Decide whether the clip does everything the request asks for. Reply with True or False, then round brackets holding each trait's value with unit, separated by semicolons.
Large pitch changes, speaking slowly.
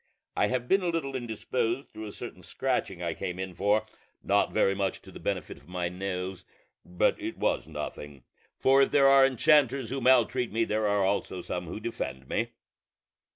False (6.2 semitones; 190 wpm)